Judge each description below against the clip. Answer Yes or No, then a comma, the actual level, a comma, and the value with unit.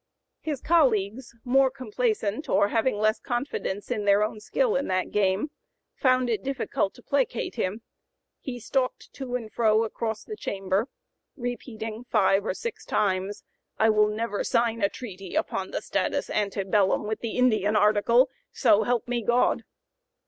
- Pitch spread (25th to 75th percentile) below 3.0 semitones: No, average, 3.4 semitones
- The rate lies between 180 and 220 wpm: No, average, 155 wpm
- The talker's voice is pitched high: Yes, high, 220 Hz